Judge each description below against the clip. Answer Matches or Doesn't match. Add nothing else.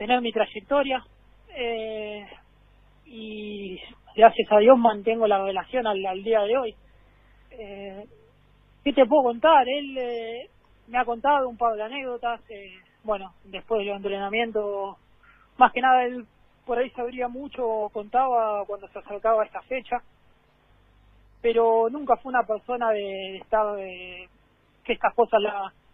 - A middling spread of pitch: Matches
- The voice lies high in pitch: Matches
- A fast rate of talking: Doesn't match